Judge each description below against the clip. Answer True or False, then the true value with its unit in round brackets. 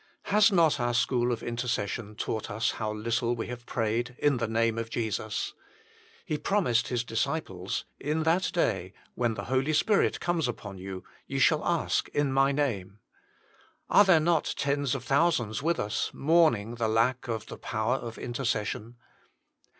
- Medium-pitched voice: False (120 Hz)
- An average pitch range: True (4.7 semitones)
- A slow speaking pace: False (165 wpm)